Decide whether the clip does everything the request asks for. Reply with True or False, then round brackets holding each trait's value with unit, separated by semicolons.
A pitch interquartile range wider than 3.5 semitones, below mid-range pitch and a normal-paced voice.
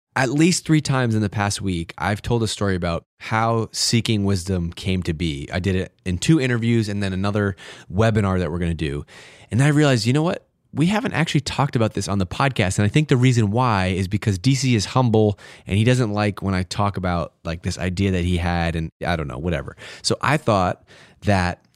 False (5.1 semitones; 100 Hz; 230 wpm)